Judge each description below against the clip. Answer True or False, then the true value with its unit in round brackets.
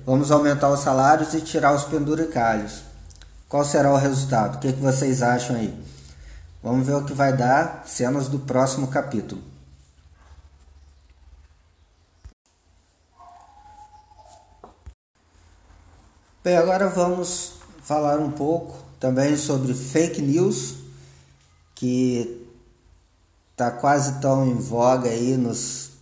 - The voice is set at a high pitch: False (125 Hz)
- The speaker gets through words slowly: True (105 wpm)